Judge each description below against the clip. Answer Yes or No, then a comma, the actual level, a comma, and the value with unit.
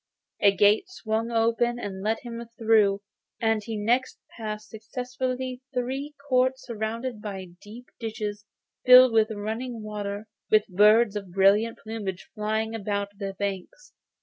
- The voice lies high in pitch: Yes, high, 220 Hz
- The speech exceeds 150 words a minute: No, slow, 135 wpm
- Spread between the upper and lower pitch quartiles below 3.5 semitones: Yes, narrow, 2.6 semitones